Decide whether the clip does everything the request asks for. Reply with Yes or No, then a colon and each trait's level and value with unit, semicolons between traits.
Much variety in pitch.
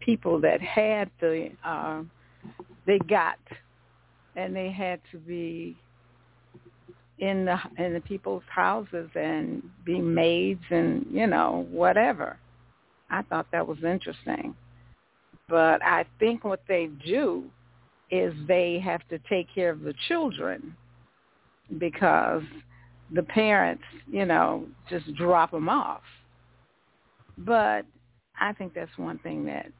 Yes: wide, 7.0 semitones